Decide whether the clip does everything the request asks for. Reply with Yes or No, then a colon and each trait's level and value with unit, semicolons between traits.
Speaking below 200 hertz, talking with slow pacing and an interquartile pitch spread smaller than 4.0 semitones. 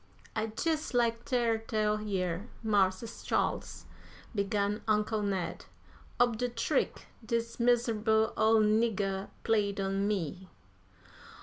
No: high, 215 Hz; slow, 110 wpm; narrow, 2.4 semitones